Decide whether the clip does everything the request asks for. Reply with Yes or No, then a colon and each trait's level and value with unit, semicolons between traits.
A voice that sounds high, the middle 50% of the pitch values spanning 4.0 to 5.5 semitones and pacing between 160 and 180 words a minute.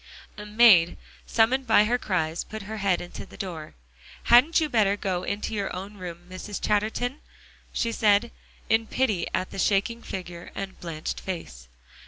No: high, 200 Hz; average, 3.6 semitones; average, 165 wpm